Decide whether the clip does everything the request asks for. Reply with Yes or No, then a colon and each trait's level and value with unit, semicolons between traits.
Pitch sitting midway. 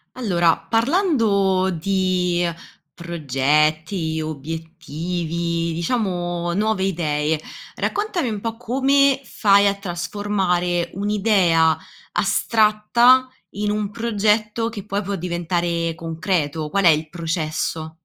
Yes: medium, 180 Hz